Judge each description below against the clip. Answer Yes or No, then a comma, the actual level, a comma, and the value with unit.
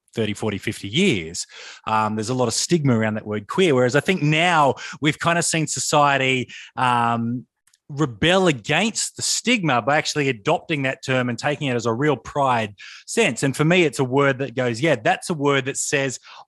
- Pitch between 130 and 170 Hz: Yes, medium, 140 Hz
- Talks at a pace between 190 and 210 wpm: Yes, average, 200 wpm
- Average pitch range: Yes, average, 4.0 semitones